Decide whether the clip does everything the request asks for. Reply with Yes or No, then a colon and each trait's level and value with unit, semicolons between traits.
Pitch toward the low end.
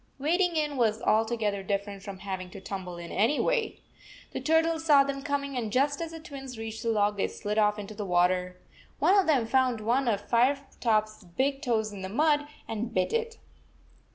No: high, 230 Hz